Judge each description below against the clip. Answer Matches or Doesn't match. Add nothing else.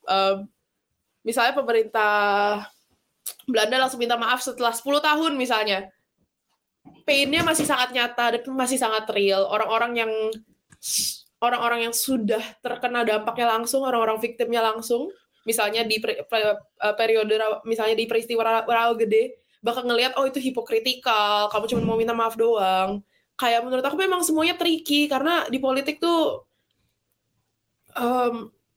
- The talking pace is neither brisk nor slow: Matches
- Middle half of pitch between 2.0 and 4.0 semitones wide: Matches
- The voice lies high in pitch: Matches